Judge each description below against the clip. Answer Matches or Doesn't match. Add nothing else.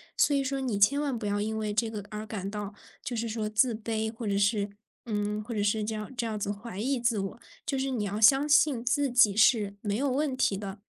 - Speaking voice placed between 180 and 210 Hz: Doesn't match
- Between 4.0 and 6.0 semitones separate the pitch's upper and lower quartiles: Doesn't match